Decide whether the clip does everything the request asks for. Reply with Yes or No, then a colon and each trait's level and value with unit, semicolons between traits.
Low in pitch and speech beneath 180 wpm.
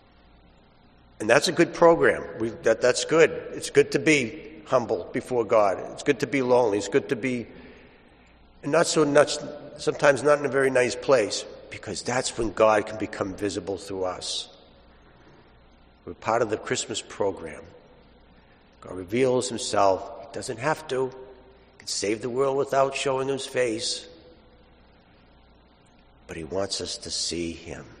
Yes: low, 120 Hz; average, 155 wpm